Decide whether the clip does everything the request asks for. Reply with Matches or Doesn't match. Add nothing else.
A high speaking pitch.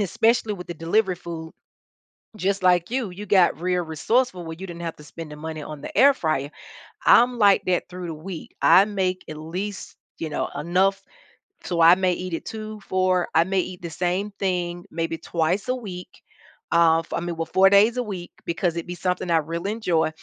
Doesn't match